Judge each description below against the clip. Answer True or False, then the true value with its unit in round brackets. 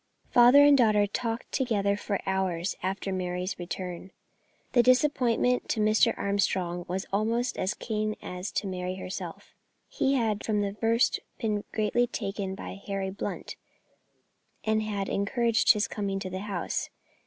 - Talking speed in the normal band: True (145 wpm)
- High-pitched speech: True (205 Hz)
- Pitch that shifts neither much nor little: True (3.2 semitones)